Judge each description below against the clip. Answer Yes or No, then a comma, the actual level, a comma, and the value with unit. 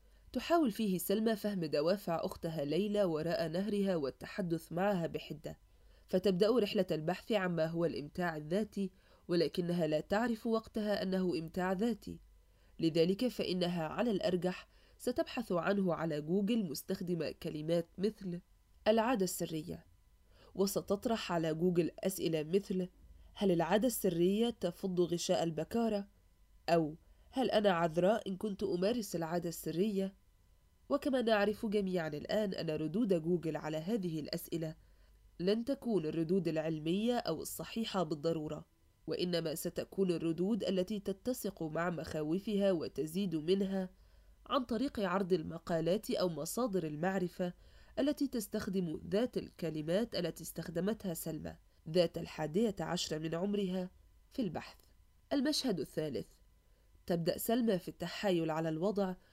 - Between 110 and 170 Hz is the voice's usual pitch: No, medium, 180 Hz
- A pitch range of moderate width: Yes, average, 4.0 semitones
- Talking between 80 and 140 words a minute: Yes, average, 115 wpm